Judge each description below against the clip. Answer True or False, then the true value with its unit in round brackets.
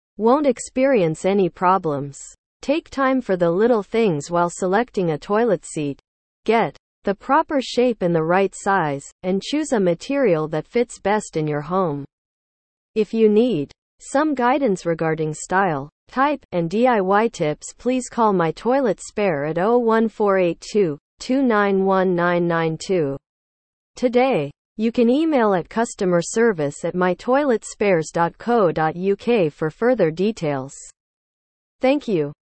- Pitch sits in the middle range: False (195 Hz)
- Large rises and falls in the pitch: True (6.3 semitones)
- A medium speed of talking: False (120 wpm)